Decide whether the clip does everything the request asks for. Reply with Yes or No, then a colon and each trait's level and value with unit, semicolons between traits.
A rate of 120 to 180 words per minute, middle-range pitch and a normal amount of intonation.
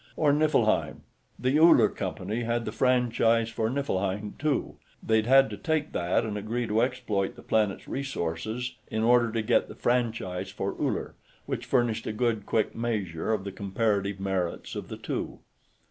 No: average, 165 wpm; low, 110 Hz; average, 3.6 semitones